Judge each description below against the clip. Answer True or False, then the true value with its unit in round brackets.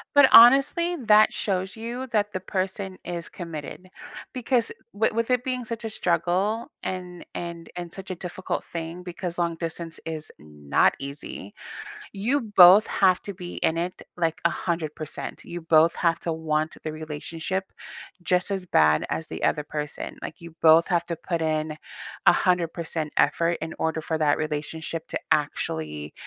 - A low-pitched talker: False (170 Hz)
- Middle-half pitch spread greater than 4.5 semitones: False (3.4 semitones)